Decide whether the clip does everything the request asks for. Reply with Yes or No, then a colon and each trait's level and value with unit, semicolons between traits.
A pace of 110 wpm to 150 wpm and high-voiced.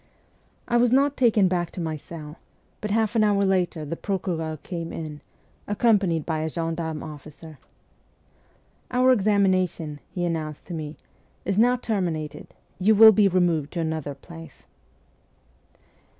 No: average, 145 wpm; medium, 175 Hz